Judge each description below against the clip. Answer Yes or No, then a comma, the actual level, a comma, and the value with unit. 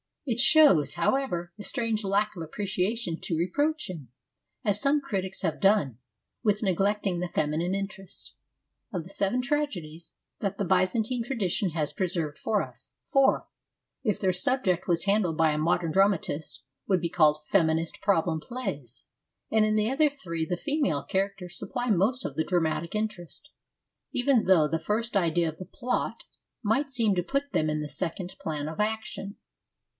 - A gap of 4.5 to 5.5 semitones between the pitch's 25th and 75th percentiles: Yes, average, 4.9 semitones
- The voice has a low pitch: No, high, 190 Hz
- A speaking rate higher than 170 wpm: No, average, 165 wpm